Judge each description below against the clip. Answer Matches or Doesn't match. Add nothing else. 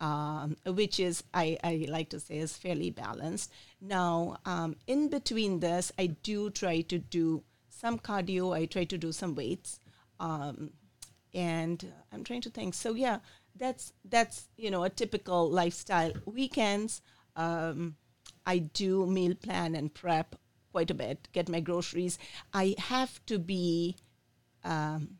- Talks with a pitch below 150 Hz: Doesn't match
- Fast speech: Doesn't match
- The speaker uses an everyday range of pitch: Matches